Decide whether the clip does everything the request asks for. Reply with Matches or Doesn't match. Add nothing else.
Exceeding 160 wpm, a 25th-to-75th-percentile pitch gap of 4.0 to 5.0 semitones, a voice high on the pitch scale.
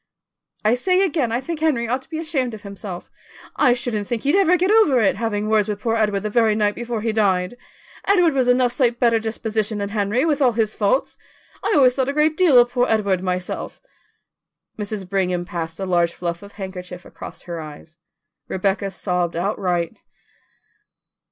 Matches